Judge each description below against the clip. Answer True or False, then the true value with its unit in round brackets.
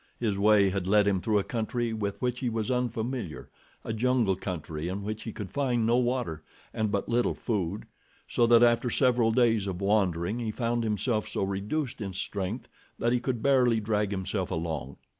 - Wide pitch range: False (3.4 semitones)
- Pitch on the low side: True (110 Hz)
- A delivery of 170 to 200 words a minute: True (190 wpm)